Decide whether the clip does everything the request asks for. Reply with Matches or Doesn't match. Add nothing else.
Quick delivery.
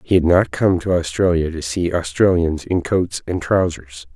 Doesn't match